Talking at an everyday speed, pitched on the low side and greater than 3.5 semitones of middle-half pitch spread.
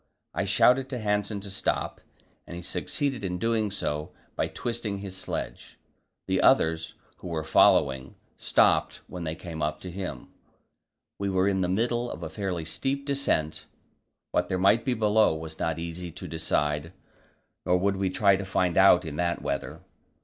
Yes: average, 170 wpm; very low, 95 Hz; average, 4.1 semitones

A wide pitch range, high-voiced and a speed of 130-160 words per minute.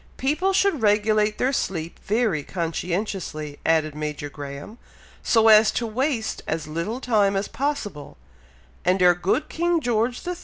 Yes: wide, 6.9 semitones; high, 210 Hz; average, 145 wpm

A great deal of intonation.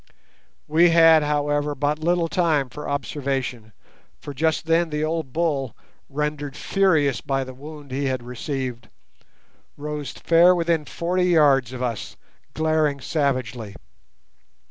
No: average, 3.2 semitones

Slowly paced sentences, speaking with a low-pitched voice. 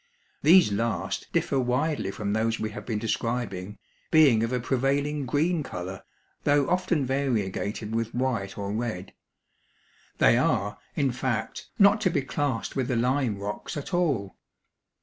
No: average, 150 wpm; low, 125 Hz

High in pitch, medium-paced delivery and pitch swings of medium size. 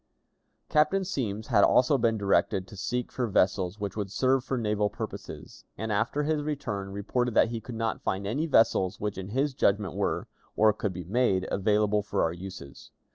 No: low, 105 Hz; average, 185 wpm; average, 4.0 semitones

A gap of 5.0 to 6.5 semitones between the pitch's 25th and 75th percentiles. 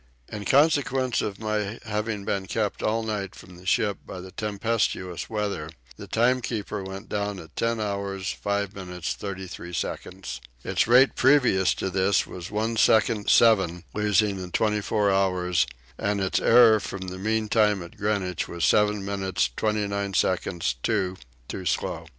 No: narrow, 2.5 semitones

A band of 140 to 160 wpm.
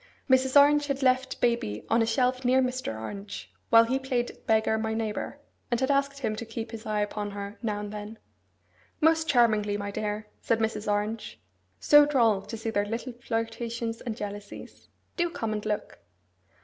No: average, 185 wpm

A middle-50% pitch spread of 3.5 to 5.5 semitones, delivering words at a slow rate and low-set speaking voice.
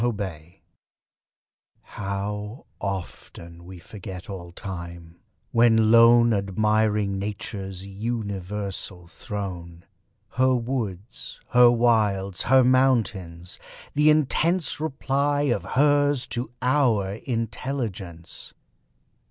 Yes: average, 4.4 semitones; slow, 85 wpm; low, 105 Hz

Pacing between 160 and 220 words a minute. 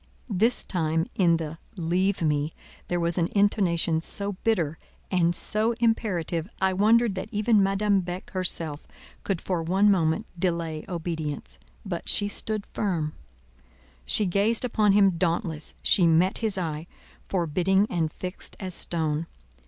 No: average, 145 wpm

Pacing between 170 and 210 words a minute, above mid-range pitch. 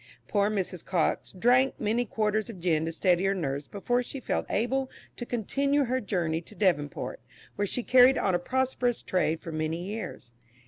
Yes: average, 180 wpm; high, 205 Hz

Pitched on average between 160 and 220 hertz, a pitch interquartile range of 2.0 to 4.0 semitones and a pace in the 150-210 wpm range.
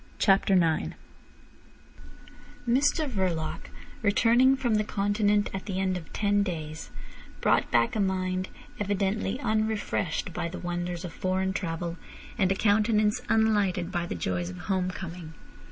No: high, 190 Hz; average, 3.3 semitones; slow, 135 wpm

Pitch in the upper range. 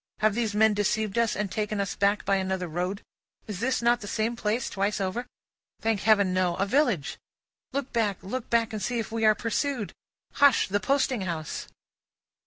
Yes: high, 210 Hz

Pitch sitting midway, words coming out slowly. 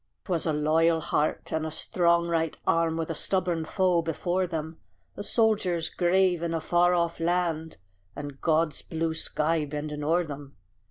No: medium, 165 Hz; average, 165 wpm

